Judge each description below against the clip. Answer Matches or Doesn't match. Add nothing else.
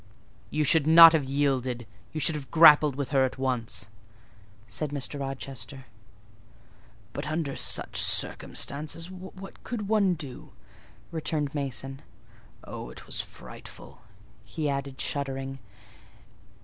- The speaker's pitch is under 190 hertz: Matches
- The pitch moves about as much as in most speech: Matches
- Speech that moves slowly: Matches